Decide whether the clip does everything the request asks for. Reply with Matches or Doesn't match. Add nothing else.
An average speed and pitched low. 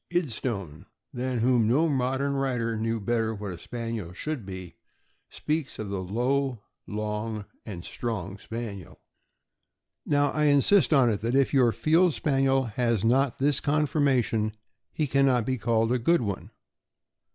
Matches